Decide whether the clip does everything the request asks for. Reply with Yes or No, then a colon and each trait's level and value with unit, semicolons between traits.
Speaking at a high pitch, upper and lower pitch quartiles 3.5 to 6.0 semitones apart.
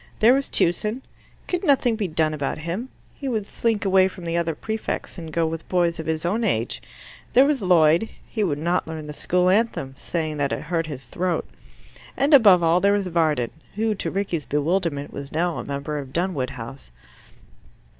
No: medium, 170 Hz; average, 4.8 semitones